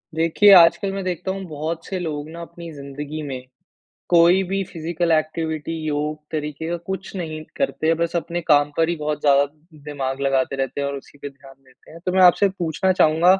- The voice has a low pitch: No, medium, 160 Hz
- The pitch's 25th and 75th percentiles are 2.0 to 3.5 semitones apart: Yes, average, 2.9 semitones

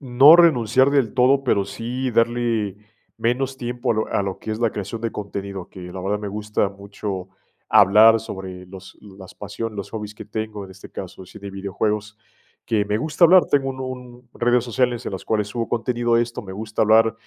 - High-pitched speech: No, low, 110 Hz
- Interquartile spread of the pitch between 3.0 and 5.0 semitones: Yes, average, 3.3 semitones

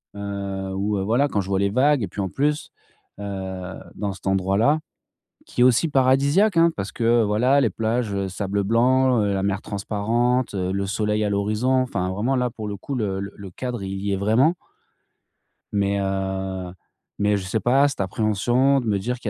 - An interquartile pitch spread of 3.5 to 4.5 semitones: Yes, average, 4.2 semitones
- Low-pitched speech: Yes, low, 105 Hz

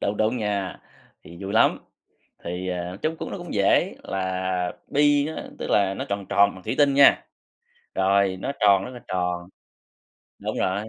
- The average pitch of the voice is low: Yes, low, 100 Hz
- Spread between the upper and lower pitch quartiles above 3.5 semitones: No, average, 2.8 semitones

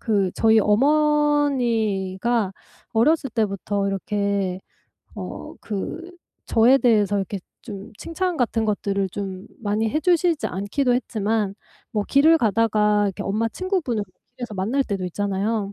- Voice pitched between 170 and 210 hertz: No, high, 220 Hz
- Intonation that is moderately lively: Yes, average, 4.5 semitones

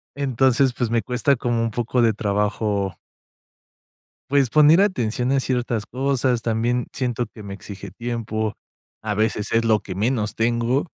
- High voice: No, low, 115 Hz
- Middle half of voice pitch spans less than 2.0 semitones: No, average, 2.8 semitones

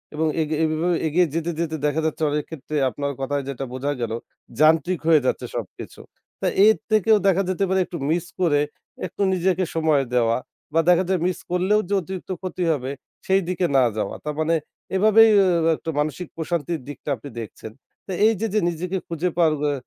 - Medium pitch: Yes, medium, 165 Hz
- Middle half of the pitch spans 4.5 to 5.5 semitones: No, average, 3.8 semitones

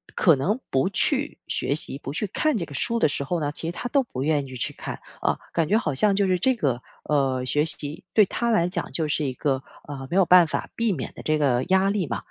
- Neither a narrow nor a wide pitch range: No, wide, 6.1 semitones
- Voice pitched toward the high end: No, medium, 155 Hz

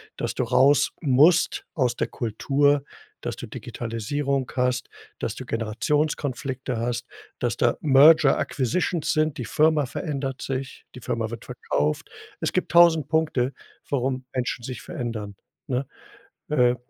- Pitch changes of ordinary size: Yes, average, 3.3 semitones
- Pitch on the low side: Yes, low, 130 Hz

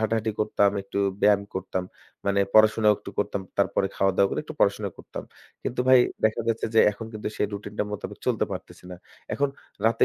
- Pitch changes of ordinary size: No, narrow, 1.8 semitones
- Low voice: Yes, low, 105 Hz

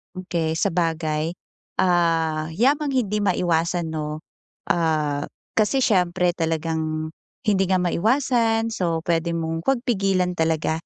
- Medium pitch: Yes, medium, 170 Hz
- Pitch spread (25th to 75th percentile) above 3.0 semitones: Yes, average, 3.5 semitones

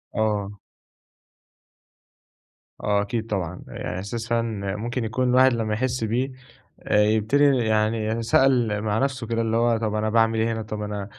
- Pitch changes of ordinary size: No, narrow, 1.8 semitones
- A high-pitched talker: No, low, 110 Hz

